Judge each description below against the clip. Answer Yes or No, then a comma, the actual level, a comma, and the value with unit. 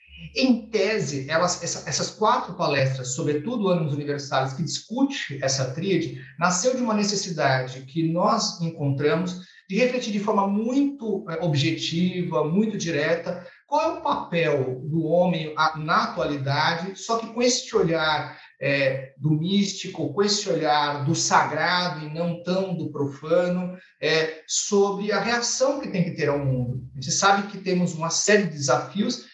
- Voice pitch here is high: No, medium, 170 Hz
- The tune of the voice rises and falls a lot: No, average, 4.9 semitones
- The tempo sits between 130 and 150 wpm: Yes, average, 145 wpm